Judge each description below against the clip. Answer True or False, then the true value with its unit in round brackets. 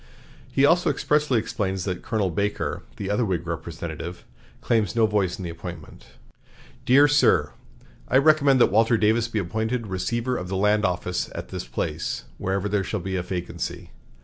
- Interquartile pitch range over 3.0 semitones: True (4.5 semitones)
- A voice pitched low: True (105 Hz)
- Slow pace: False (170 wpm)